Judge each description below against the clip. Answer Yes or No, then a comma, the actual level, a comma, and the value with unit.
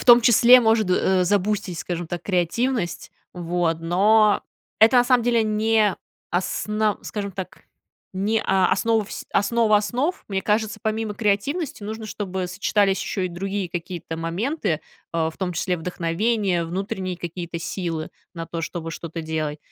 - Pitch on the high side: Yes, high, 195 Hz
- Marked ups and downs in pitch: No, average, 3.9 semitones